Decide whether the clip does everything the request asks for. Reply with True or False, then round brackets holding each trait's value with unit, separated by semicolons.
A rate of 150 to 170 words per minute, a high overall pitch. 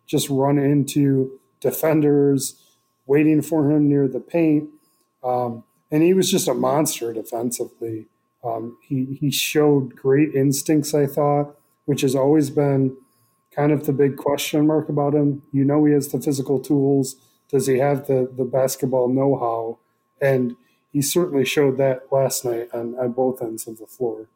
False (165 wpm; 140 Hz)